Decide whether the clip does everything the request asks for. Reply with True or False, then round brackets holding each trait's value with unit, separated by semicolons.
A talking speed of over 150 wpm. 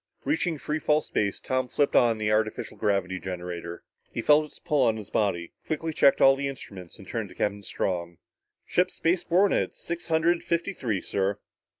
True (190 wpm)